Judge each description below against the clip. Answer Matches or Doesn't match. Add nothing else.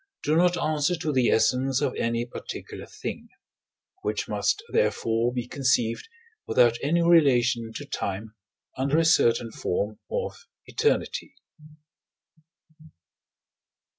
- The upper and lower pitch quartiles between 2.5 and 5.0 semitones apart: Doesn't match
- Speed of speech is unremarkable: Doesn't match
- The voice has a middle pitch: Doesn't match